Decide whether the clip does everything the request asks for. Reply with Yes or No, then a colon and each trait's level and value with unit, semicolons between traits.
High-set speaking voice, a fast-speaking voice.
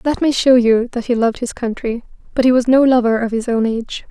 Yes: high, 240 Hz; fast, 265 wpm